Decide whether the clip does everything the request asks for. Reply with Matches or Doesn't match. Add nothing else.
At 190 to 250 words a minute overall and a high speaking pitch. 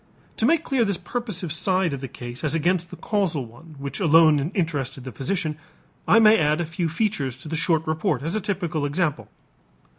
Doesn't match